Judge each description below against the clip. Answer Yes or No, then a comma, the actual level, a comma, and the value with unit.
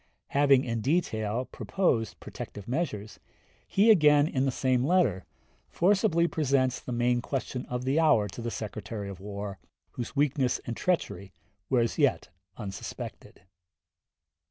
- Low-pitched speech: Yes, low, 125 Hz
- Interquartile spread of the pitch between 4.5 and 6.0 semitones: Yes, average, 5.3 semitones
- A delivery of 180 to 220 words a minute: No, slow, 135 wpm